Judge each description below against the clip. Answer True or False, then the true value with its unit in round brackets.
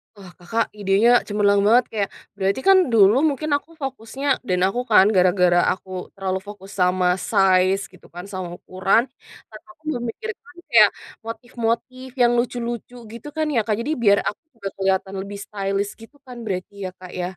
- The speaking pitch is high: True (205 Hz)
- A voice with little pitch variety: False (3.8 semitones)